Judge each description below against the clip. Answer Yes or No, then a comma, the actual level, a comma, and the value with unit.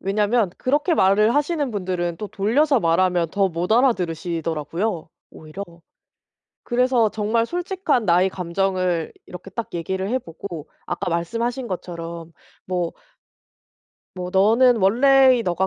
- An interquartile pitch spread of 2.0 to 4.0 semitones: No, wide, 5.5 semitones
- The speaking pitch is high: Yes, high, 195 Hz